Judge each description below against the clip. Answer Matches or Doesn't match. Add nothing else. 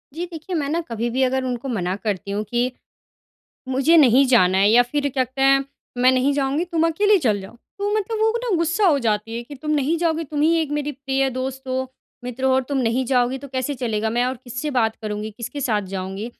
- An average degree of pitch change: Matches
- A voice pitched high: Matches